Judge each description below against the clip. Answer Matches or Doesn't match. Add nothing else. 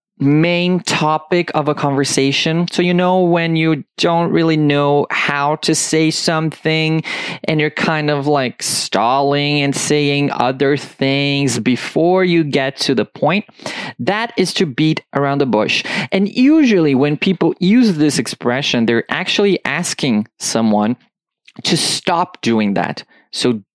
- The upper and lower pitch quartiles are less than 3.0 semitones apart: Doesn't match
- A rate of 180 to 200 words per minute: Doesn't match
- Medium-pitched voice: Matches